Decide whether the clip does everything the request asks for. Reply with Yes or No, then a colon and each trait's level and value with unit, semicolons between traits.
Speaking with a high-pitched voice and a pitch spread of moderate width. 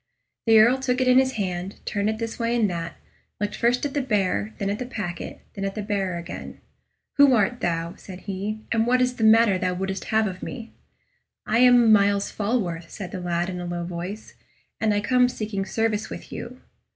Yes: high, 210 Hz; average, 3.9 semitones